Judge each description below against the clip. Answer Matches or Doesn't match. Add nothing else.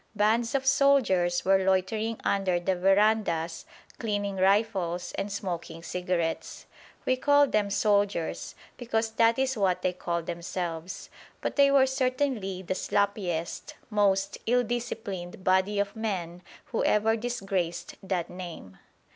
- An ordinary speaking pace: Doesn't match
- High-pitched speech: Matches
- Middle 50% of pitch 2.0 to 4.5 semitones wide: Matches